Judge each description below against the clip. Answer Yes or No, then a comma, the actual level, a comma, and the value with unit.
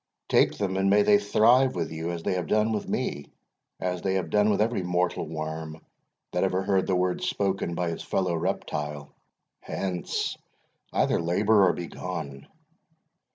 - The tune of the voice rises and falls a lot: No, average, 3.3 semitones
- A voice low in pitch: Yes, very low, 90 Hz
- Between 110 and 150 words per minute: No, average, 165 wpm